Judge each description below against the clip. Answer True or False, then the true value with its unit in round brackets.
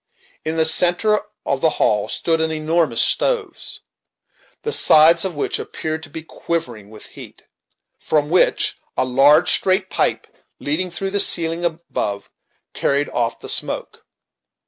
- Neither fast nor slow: True (145 wpm)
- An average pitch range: True (3.2 semitones)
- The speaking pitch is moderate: True (160 Hz)